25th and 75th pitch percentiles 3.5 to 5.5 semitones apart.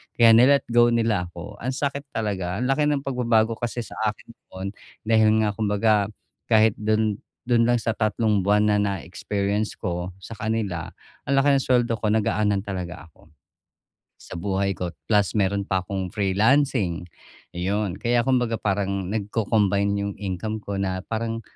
No: average, 2.9 semitones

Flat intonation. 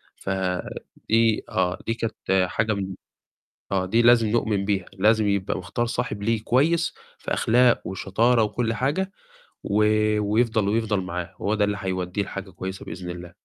No: average, 3.3 semitones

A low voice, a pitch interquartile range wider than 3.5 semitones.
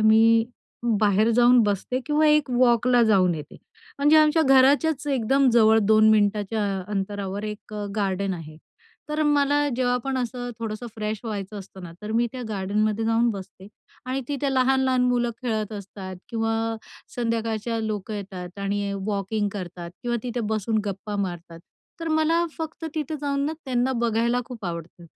No: high, 225 Hz; average, 4.0 semitones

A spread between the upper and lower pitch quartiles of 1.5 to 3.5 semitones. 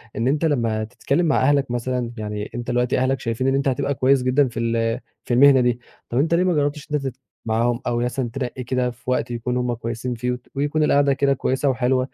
Yes: narrow, 2.5 semitones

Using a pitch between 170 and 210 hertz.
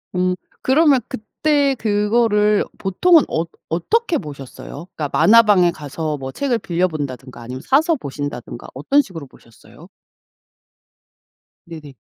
Yes: medium, 185 Hz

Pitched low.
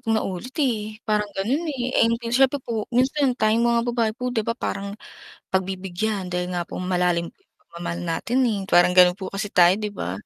No: high, 215 Hz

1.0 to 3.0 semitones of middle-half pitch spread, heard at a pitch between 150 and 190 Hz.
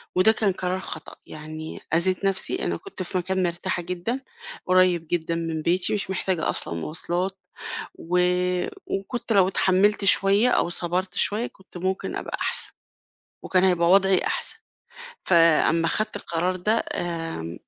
Yes: narrow, 2.4 semitones; medium, 185 Hz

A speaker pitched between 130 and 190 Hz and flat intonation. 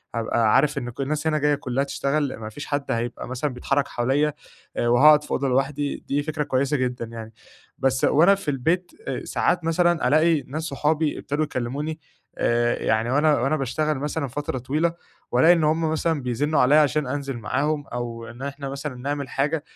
No: medium, 140 Hz; average, 3.3 semitones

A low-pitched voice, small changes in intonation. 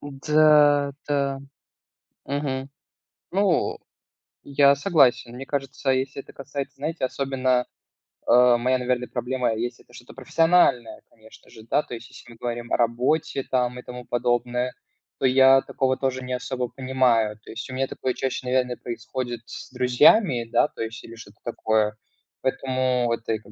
Yes: low, 130 Hz; narrow, 2.0 semitones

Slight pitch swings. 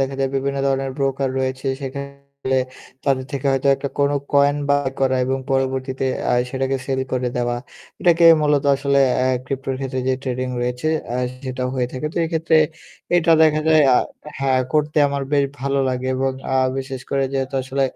Yes: narrow, 1.3 semitones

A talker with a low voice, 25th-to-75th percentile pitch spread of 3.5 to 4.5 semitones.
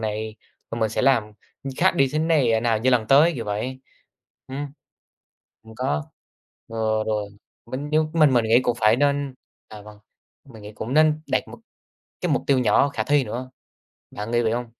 Yes: low, 120 Hz; average, 4.0 semitones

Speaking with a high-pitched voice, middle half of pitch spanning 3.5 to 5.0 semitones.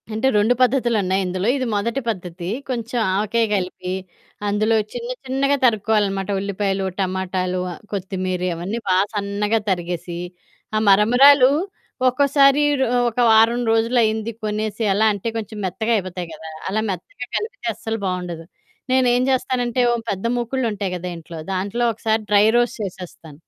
Yes: high, 210 Hz; average, 4.3 semitones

